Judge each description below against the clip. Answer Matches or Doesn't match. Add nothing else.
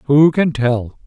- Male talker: Matches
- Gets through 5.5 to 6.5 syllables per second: Doesn't match